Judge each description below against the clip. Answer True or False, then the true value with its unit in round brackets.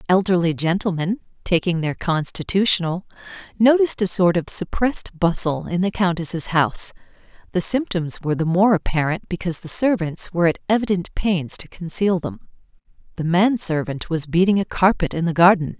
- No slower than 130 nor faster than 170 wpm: True (155 wpm)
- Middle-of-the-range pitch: True (180 Hz)